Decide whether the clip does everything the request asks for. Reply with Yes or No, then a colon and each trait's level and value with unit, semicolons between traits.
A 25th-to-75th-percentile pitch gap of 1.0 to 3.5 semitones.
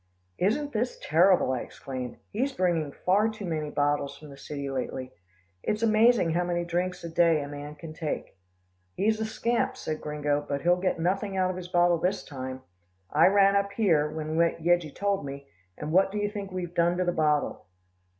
No: average, 4.8 semitones